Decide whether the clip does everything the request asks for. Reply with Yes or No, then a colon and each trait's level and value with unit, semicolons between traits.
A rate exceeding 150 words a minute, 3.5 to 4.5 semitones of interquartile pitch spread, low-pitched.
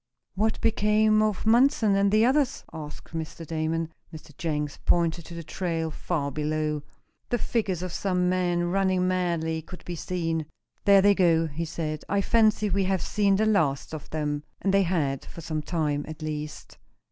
No: average, 175 wpm; average, 3.9 semitones; medium, 175 Hz